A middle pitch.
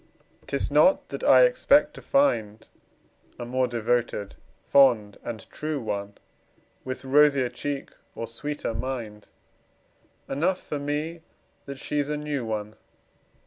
No: low, 130 Hz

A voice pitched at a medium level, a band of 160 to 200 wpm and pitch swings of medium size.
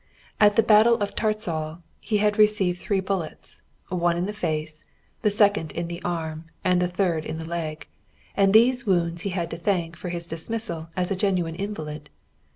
Yes: medium, 180 Hz; average, 185 wpm; average, 3.8 semitones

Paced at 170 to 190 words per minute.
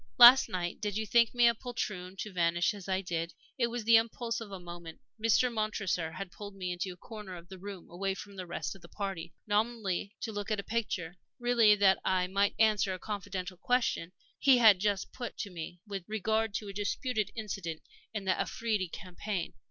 No: fast, 205 wpm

